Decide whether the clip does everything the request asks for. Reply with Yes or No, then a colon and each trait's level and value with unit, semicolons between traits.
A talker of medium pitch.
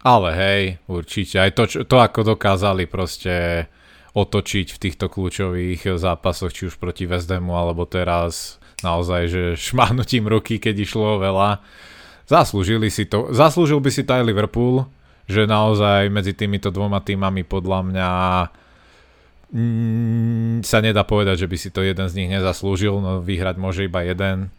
No: very low, 95 Hz